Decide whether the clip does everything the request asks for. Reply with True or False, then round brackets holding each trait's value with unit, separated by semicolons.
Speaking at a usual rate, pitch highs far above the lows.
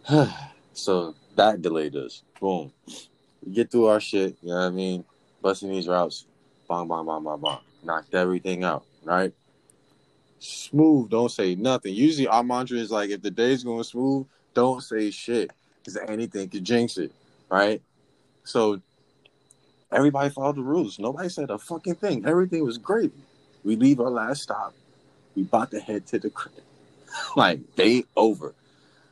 True (160 wpm; 6.5 semitones)